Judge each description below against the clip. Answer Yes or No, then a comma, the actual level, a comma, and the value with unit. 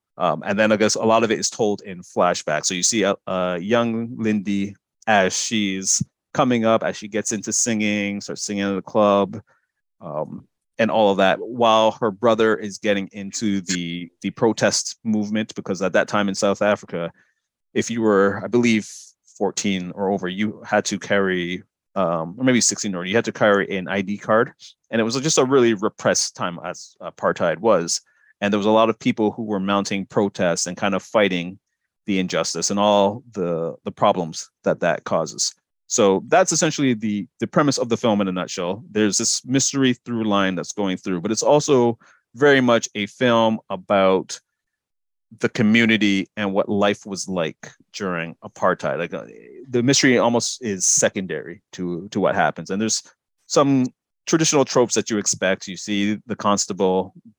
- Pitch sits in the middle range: No, low, 105 Hz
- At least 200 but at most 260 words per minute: No, average, 185 wpm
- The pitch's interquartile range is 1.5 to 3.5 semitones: Yes, average, 2.7 semitones